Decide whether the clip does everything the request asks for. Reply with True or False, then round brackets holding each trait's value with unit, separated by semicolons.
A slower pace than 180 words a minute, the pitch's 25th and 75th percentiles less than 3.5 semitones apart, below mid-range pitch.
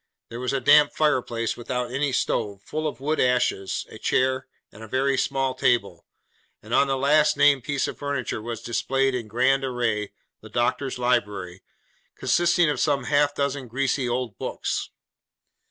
True (165 wpm; 2.9 semitones; 130 Hz)